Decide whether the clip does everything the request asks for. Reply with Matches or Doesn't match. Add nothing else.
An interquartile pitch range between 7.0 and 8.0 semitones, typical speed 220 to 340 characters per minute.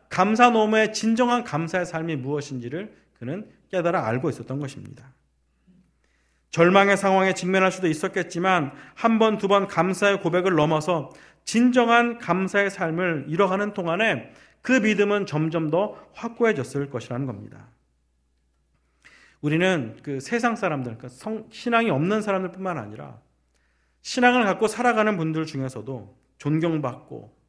Matches